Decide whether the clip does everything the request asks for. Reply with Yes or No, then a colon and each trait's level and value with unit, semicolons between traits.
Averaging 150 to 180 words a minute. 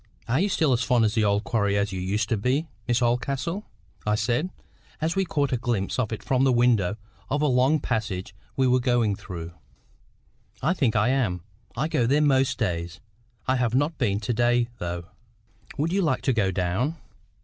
No: average, 200 wpm